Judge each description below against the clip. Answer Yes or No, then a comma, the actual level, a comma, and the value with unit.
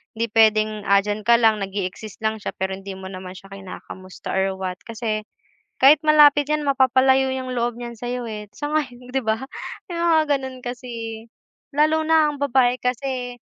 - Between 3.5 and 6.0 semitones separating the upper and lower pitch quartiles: Yes, average, 4.1 semitones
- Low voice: No, high, 240 Hz